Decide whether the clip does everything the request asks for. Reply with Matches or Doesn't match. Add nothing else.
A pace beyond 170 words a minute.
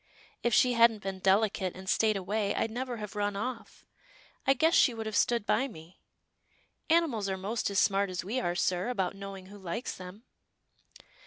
Matches